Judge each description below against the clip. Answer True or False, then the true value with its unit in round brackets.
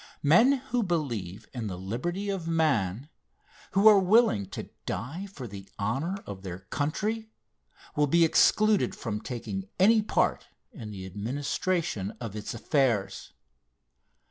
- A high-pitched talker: False (145 Hz)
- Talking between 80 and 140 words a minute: True (135 wpm)